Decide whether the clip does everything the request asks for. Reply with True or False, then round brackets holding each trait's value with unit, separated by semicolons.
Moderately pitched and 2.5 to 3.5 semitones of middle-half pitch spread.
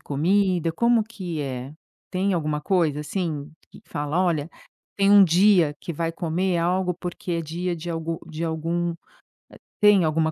True (170 Hz; 2.8 semitones)